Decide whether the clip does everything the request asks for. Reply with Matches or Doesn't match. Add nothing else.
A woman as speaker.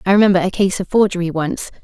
Matches